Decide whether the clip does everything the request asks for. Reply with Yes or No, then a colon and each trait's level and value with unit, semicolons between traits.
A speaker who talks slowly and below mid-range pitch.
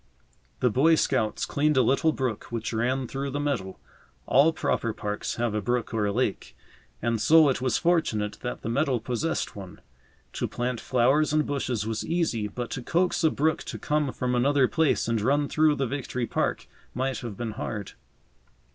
No: average, 185 wpm; low, 125 Hz